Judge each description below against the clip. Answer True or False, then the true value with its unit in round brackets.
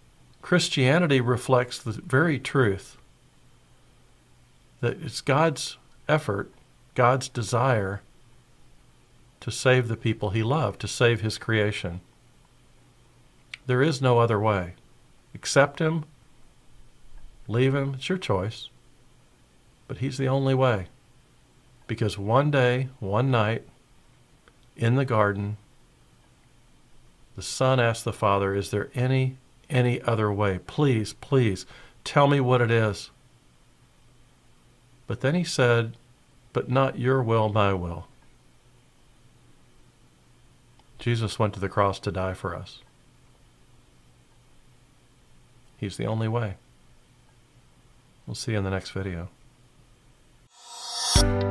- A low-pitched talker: True (120 Hz)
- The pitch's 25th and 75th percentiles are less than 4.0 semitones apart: False (4.3 semitones)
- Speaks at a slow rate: True (110 wpm)